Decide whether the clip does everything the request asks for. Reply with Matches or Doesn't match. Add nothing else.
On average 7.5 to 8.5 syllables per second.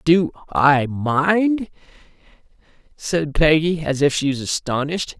Doesn't match